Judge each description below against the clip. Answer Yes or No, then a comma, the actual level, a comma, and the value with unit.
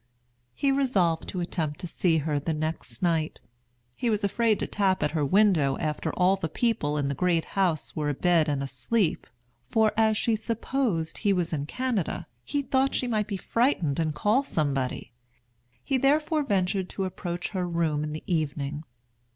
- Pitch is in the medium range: Yes, medium, 180 Hz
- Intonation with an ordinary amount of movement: No, wide, 6.0 semitones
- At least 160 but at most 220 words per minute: Yes, average, 175 wpm